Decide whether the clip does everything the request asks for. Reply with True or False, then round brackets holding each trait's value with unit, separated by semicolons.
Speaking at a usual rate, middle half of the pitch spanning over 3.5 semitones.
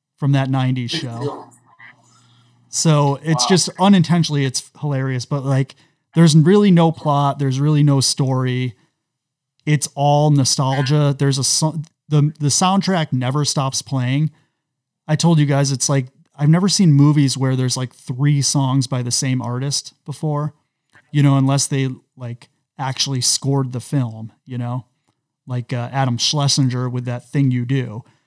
False (150 wpm; 2.7 semitones)